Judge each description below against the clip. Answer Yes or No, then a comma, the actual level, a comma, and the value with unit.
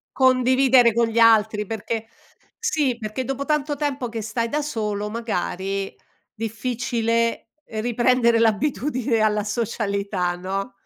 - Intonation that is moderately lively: Yes, average, 3.2 semitones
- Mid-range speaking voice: No, high, 230 Hz